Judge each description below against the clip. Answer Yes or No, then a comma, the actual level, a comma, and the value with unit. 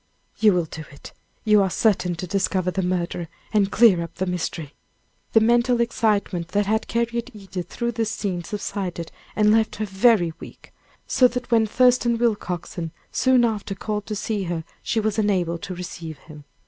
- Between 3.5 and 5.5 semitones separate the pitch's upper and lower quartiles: Yes, average, 4.0 semitones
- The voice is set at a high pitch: Yes, high, 205 Hz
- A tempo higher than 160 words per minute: Yes, average, 175 wpm